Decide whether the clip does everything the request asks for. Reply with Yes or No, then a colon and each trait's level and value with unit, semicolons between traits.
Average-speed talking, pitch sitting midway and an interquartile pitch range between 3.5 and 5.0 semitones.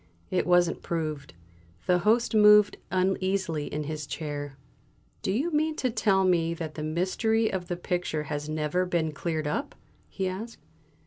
Yes: average, 155 wpm; medium, 175 Hz; average, 4.3 semitones